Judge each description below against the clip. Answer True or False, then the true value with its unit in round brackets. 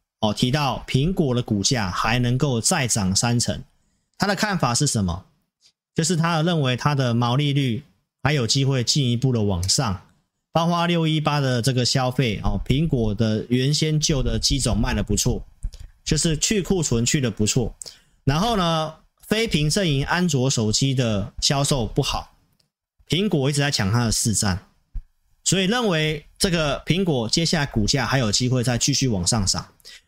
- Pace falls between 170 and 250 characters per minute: True (245 characters per minute)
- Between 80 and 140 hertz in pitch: True (135 Hz)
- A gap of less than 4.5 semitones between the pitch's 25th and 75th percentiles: False (5.4 semitones)